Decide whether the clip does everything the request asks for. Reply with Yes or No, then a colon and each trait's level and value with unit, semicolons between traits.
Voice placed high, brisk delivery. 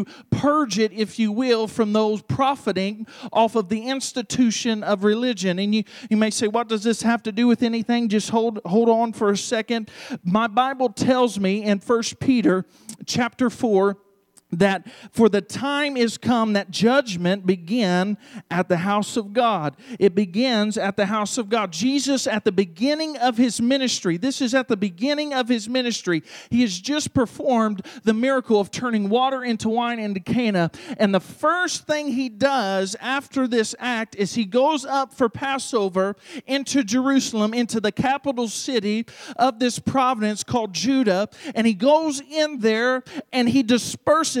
No: high, 230 Hz; average, 170 wpm